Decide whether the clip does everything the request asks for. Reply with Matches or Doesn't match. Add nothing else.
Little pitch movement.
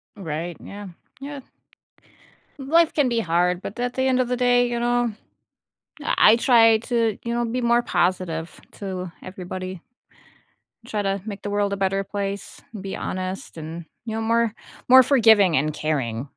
Doesn't match